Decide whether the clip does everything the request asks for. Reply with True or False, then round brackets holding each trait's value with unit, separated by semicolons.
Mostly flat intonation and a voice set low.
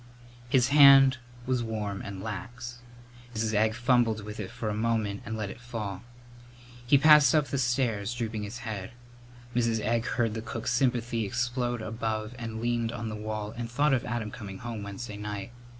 True (2.3 semitones; 115 Hz)